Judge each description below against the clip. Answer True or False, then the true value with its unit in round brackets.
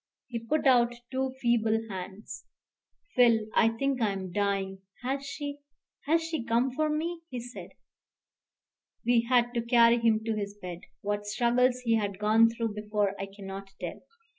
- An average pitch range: True (3.4 semitones)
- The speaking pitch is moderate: False (230 Hz)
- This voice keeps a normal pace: True (165 wpm)